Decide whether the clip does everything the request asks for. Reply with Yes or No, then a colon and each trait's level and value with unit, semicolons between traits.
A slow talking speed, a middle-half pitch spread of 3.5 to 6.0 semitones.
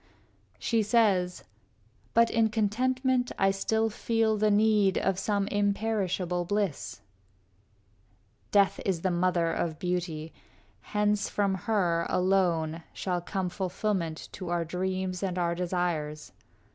No: slow, 120 wpm; average, 3.1 semitones